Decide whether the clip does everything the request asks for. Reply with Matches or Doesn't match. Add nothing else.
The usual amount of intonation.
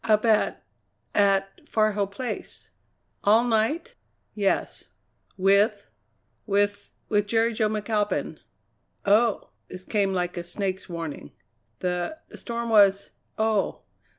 Doesn't match